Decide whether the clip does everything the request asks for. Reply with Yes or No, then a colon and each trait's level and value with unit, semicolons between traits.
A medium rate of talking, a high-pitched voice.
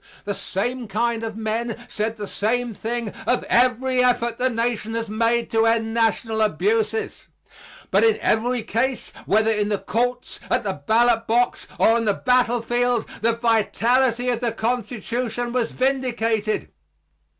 Yes: average, 150 wpm; high, 230 Hz